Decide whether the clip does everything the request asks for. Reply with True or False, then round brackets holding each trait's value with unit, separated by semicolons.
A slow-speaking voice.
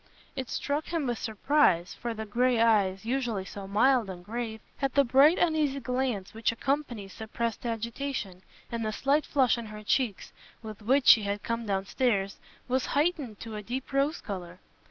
False (175 wpm)